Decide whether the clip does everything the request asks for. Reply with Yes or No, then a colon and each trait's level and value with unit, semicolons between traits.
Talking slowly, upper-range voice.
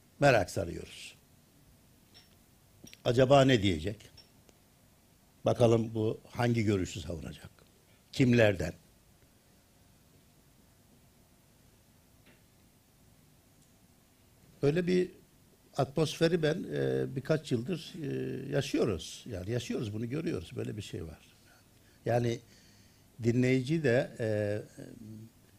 No: slow, 75 wpm; low, 120 Hz